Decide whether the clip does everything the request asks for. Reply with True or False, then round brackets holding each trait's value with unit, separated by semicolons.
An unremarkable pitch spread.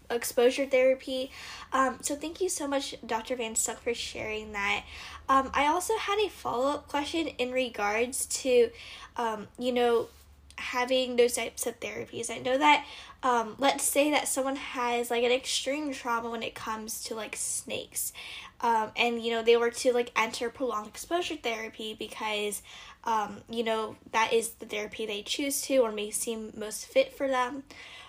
True (3.0 semitones)